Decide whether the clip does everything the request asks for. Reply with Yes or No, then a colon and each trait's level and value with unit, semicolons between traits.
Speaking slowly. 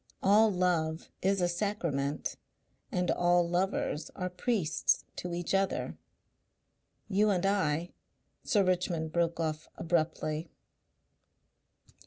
Yes: slow, 110 wpm